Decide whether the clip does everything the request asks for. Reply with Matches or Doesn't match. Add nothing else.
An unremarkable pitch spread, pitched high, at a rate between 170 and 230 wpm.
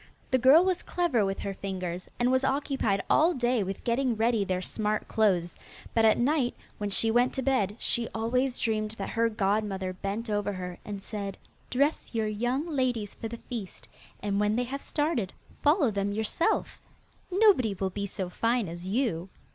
Matches